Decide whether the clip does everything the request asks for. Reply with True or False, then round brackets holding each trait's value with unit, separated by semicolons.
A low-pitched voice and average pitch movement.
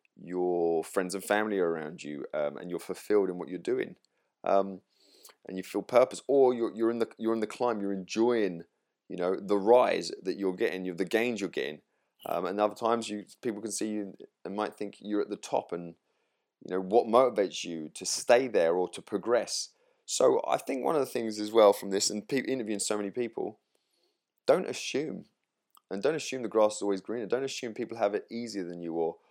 True (105 Hz; 3.6 semitones)